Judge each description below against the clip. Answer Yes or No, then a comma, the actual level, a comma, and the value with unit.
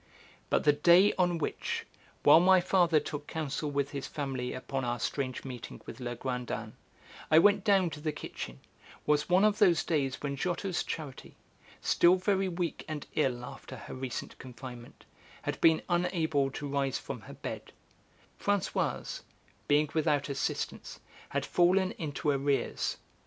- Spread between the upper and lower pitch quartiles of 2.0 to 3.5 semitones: No, average, 4.5 semitones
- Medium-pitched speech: Yes, medium, 150 Hz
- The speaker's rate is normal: Yes, average, 150 wpm